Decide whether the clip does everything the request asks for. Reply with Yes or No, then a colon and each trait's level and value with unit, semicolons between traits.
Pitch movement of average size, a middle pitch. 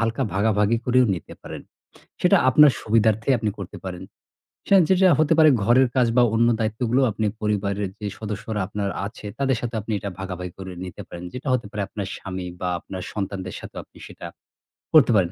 No: average, 3.8 semitones; low, 105 Hz